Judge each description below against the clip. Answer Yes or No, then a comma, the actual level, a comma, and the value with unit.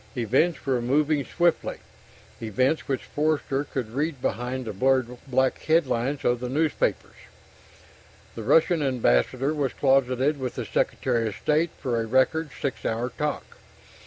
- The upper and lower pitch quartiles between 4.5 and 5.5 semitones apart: No, average, 3.4 semitones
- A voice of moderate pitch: No, low, 130 Hz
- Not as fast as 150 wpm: Yes, average, 140 wpm